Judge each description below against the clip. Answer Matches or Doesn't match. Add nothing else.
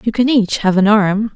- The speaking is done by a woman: Matches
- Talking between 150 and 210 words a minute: Doesn't match